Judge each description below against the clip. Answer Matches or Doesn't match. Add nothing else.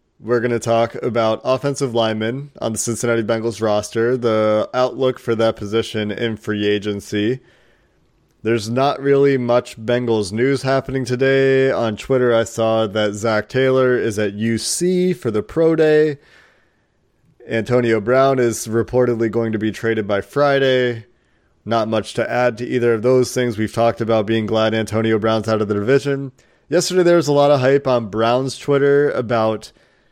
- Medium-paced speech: Matches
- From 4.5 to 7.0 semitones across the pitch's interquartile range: Doesn't match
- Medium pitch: Doesn't match